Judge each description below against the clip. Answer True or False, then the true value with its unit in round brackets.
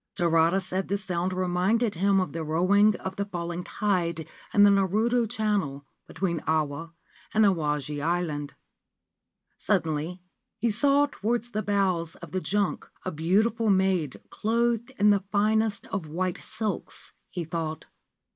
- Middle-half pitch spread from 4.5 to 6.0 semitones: False (3.9 semitones)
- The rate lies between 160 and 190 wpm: False (140 wpm)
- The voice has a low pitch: False (190 Hz)